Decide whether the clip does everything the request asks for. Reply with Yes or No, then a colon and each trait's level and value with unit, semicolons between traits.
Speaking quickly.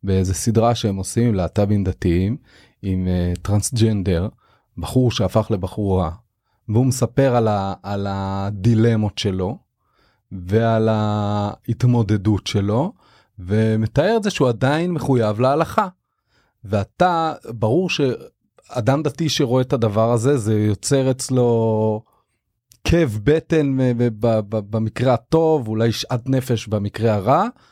No: average, 105 wpm